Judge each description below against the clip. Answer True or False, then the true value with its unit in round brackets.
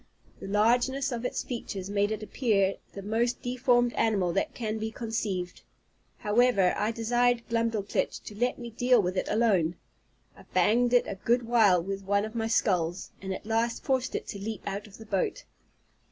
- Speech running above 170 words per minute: True (180 wpm)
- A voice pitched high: True (220 Hz)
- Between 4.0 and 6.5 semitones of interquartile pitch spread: False (3.3 semitones)